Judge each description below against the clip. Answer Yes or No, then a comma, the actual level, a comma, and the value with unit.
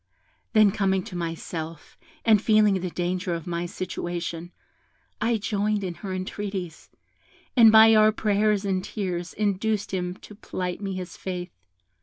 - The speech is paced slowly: No, average, 145 wpm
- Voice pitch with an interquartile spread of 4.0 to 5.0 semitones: No, average, 3.0 semitones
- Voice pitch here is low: No, high, 190 Hz